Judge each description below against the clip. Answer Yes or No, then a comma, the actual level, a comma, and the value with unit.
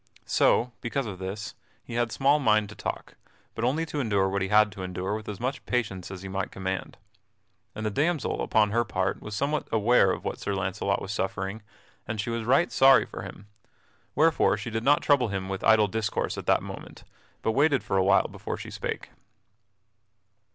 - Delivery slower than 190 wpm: No, average, 200 wpm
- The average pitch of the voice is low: Yes, low, 110 Hz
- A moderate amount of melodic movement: Yes, average, 4.1 semitones